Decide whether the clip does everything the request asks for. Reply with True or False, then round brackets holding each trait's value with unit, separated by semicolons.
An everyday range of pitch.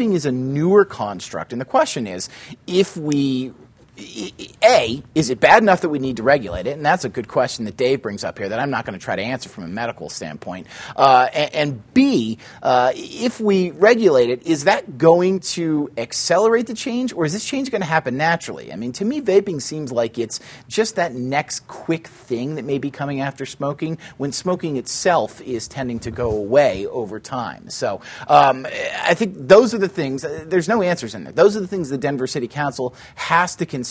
False (6.5 semitones)